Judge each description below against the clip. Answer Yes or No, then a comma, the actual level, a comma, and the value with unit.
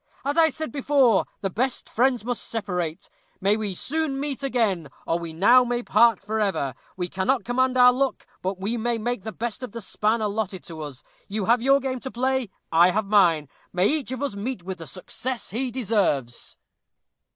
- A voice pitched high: Yes, high, 225 Hz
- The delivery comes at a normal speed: Yes, average, 195 wpm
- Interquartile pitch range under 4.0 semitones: No, average, 5.3 semitones